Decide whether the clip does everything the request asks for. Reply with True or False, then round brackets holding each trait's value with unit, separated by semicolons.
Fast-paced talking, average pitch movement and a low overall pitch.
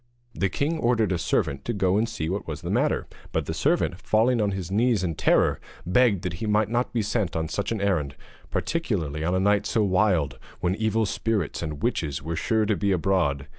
True (215 wpm; 4.5 semitones; 100 Hz)